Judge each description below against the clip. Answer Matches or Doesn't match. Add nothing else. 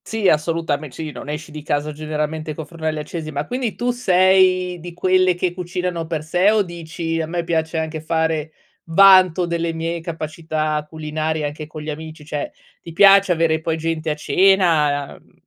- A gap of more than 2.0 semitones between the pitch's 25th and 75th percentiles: Matches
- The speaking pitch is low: Doesn't match